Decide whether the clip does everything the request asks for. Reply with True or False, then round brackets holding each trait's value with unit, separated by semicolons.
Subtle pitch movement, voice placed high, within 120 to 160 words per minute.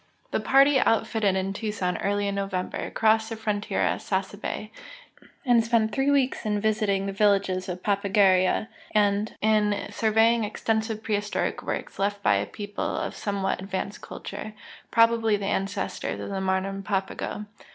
True (2.0 semitones; 205 Hz; 155 wpm)